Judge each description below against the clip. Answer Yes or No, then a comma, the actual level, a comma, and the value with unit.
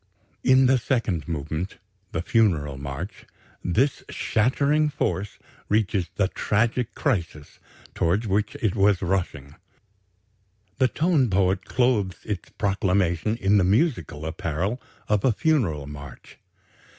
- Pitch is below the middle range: Yes, low, 100 Hz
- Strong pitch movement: Yes, wide, 5.8 semitones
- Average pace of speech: No, slow, 115 wpm